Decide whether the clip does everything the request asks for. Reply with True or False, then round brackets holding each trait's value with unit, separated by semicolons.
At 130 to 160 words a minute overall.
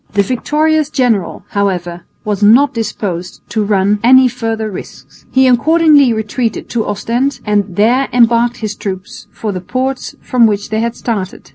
True (155 wpm)